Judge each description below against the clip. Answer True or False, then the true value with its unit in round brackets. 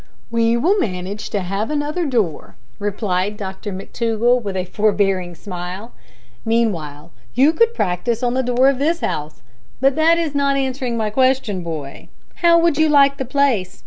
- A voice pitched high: True (230 Hz)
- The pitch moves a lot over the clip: True (6.5 semitones)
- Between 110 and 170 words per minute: True (165 wpm)